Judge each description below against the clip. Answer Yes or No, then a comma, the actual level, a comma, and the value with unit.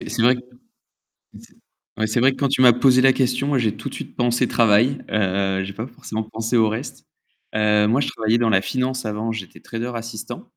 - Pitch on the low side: Yes, low, 115 Hz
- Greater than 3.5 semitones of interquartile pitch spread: No, average, 2.8 semitones